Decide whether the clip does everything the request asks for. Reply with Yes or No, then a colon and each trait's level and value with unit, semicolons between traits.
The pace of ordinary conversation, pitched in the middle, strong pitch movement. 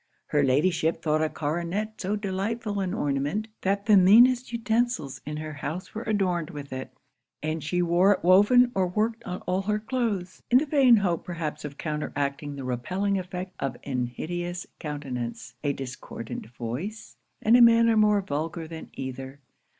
Yes: average, 165 wpm; medium, 180 Hz; wide, 6.2 semitones